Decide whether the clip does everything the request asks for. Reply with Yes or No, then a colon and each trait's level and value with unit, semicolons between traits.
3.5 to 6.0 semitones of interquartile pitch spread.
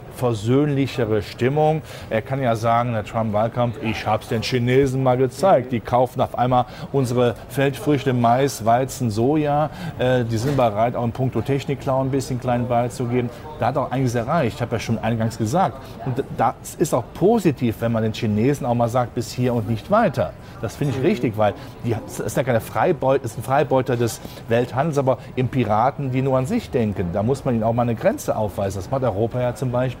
No: narrow, 2.6 semitones